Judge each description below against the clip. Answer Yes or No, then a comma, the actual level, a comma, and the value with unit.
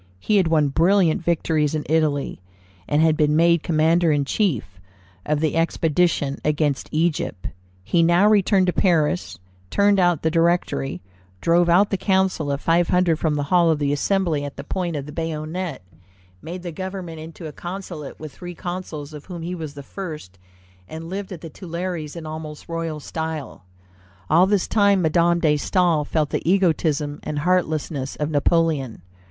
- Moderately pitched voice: Yes, medium, 165 Hz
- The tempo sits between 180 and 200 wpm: No, average, 170 wpm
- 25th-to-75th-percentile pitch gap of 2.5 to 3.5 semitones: Yes, average, 2.8 semitones